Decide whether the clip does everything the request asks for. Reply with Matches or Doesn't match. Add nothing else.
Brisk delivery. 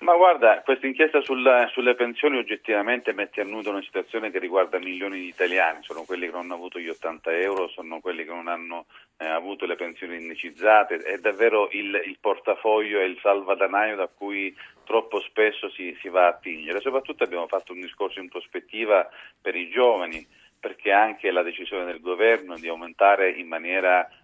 Matches